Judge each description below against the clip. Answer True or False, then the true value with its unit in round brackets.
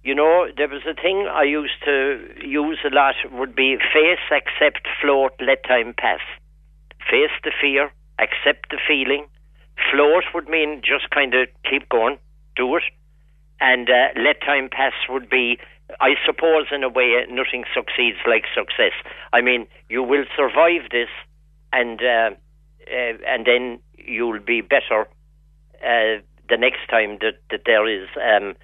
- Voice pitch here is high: False (140 Hz)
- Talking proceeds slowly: False (155 wpm)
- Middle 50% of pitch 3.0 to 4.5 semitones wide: True (3.4 semitones)